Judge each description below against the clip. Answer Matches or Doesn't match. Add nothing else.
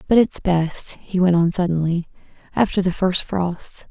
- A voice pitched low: Doesn't match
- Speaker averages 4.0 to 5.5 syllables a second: Matches